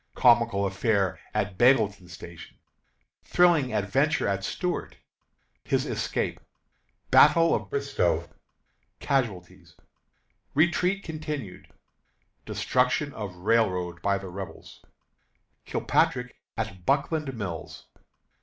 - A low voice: Yes, low, 110 Hz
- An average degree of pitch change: No, wide, 7.1 semitones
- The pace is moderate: No, slow, 90 wpm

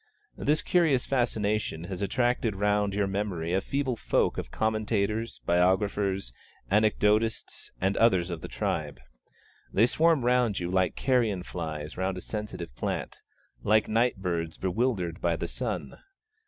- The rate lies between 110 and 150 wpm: Yes, average, 140 wpm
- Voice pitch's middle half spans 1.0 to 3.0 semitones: No, average, 3.9 semitones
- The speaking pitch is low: Yes, low, 105 Hz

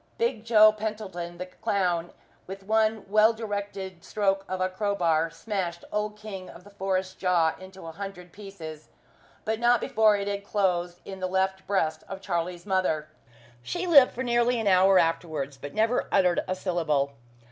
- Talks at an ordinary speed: Yes, average, 170 wpm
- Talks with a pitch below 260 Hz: Yes, high, 190 Hz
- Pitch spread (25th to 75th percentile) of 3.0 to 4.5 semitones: Yes, average, 3.3 semitones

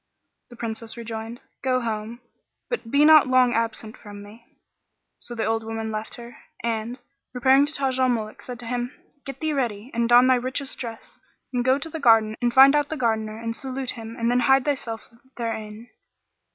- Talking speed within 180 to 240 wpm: Yes, average, 190 wpm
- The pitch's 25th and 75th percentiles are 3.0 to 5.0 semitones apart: No, narrow, 2.6 semitones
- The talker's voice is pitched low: No, high, 240 Hz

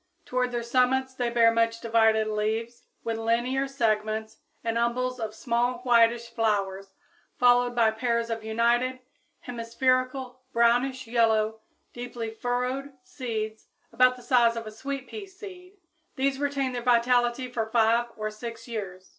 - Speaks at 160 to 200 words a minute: No, average, 140 wpm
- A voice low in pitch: No, high, 235 Hz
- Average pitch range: No, narrow, 2.0 semitones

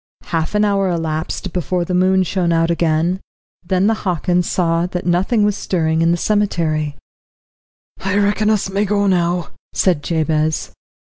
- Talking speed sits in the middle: Yes, average, 155 wpm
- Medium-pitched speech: Yes, medium, 180 Hz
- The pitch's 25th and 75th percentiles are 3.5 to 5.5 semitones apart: No, average, 2.7 semitones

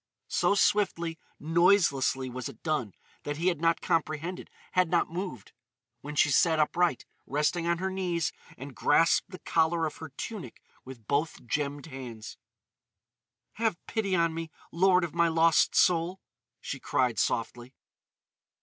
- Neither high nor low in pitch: Yes, medium, 165 Hz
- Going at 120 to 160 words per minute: Yes, average, 140 wpm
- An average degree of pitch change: Yes, average, 3.7 semitones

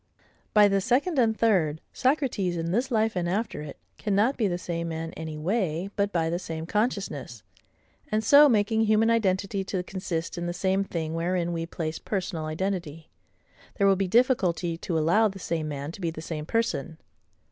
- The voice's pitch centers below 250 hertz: Yes, medium, 185 Hz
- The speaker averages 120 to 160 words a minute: No, average, 185 wpm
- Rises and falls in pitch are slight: No, average, 4.6 semitones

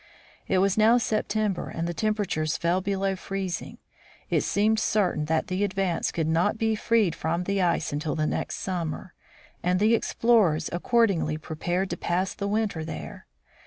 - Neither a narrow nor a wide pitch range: Yes, average, 3.9 semitones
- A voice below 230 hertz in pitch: Yes, medium, 185 Hz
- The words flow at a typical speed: Yes, average, 165 wpm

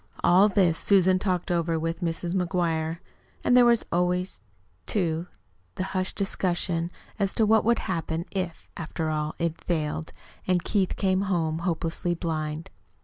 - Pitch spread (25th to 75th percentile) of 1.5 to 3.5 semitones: Yes, narrow, 2.4 semitones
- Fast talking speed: No, average, 145 wpm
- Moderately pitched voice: Yes, medium, 175 Hz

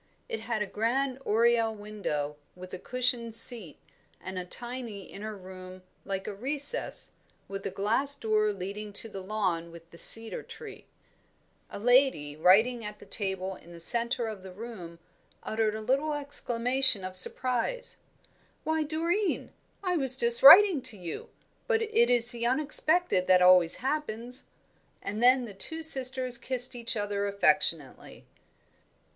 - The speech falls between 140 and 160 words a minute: Yes, average, 150 wpm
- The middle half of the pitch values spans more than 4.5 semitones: Yes, average, 5.2 semitones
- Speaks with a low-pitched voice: No, high, 225 Hz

